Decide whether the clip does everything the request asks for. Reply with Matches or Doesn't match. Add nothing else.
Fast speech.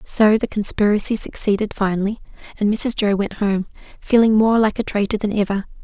Doesn't match